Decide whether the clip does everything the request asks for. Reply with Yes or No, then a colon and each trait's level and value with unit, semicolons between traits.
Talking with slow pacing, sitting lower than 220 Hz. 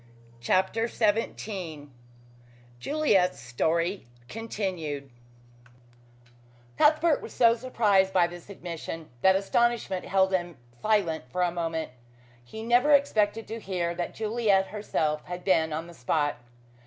Yes: slow, 115 wpm; high, 190 Hz